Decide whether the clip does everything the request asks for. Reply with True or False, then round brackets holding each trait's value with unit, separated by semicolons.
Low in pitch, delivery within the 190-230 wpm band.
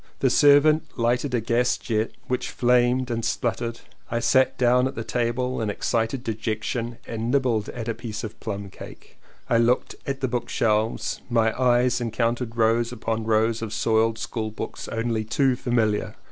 False (115 Hz; 175 wpm)